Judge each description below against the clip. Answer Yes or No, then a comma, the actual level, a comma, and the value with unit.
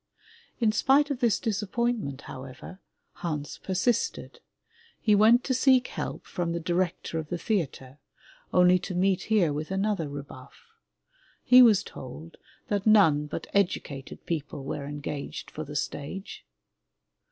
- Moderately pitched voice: Yes, medium, 180 Hz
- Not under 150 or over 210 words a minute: No, slow, 135 wpm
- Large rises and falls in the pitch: Yes, wide, 6.5 semitones